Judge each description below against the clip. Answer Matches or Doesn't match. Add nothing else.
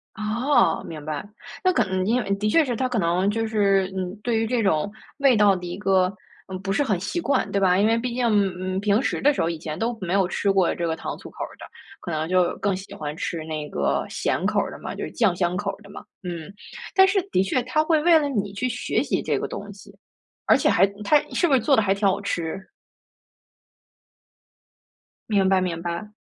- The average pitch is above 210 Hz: Doesn't match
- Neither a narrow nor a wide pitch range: Matches